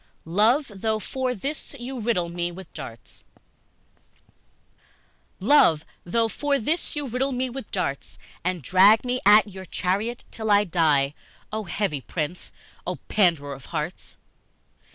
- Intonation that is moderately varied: No, wide, 6.1 semitones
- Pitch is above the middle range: Yes, high, 205 Hz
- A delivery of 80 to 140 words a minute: Yes, slow, 135 wpm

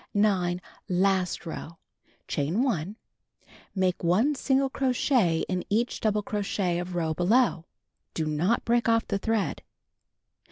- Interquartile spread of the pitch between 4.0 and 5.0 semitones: Yes, average, 4.6 semitones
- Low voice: No, high, 195 Hz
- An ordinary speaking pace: No, slow, 125 wpm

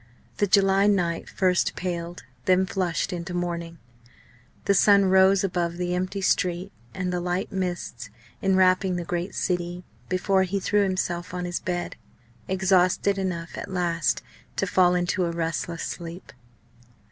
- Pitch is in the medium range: Yes, medium, 180 Hz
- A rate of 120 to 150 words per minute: Yes, average, 145 wpm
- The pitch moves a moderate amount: No, narrow, 1.5 semitones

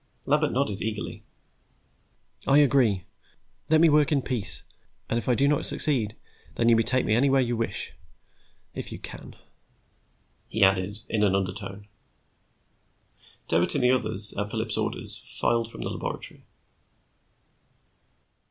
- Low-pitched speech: Yes, low, 115 Hz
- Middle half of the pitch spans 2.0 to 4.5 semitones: No, average, 4.9 semitones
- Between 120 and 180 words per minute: Yes, average, 140 wpm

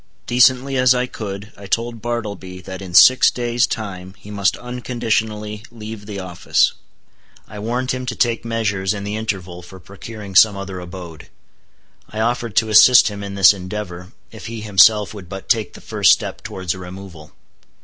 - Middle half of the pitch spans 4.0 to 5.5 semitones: No, average, 3.3 semitones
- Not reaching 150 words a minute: No, average, 175 wpm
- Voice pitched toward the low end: Yes, low, 105 Hz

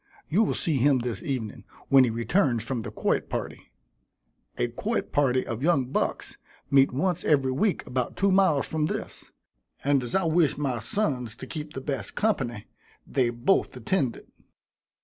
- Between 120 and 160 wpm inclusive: No, average, 170 wpm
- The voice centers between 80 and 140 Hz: Yes, low, 135 Hz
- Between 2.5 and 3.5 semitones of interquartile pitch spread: No, average, 5.0 semitones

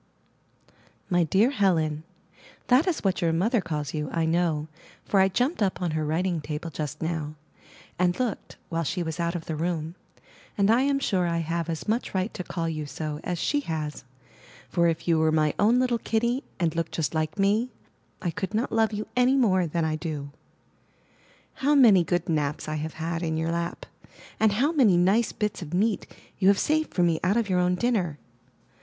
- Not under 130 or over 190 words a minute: No, average, 200 wpm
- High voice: No, medium, 175 Hz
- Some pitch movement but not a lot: Yes, average, 4.9 semitones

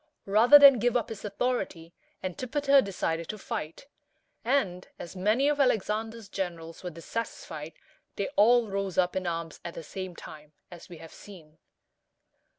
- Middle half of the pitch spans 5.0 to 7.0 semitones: Yes, wide, 5.6 semitones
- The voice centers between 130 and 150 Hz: No, high, 195 Hz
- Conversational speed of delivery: Yes, average, 155 wpm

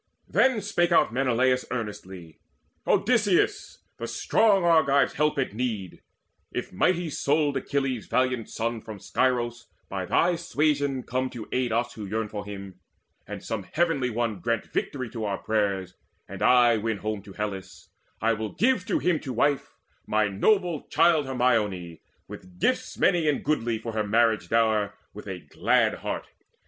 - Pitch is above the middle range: No, low, 120 Hz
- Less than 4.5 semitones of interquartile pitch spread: No, wide, 5.4 semitones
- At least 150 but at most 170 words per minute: Yes, average, 155 wpm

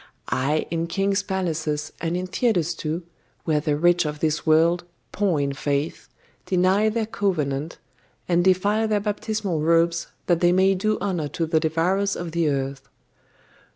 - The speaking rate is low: No, average, 155 wpm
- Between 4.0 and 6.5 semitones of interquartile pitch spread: No, average, 3.6 semitones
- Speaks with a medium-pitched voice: Yes, medium, 170 Hz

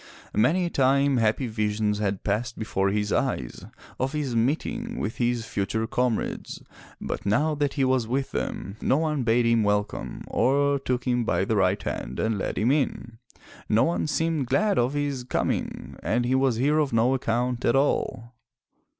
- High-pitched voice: No, low, 125 Hz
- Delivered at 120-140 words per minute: No, average, 180 wpm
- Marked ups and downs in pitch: No, average, 3.9 semitones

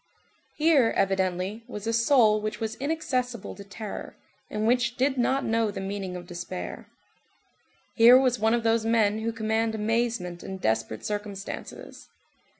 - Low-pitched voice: No, high, 220 Hz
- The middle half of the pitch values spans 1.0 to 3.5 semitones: Yes, average, 3.1 semitones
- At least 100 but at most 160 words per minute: Yes, average, 150 wpm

